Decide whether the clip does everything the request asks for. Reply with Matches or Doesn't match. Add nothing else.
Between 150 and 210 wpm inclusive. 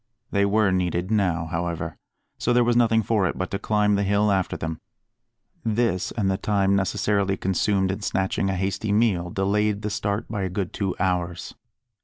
Matches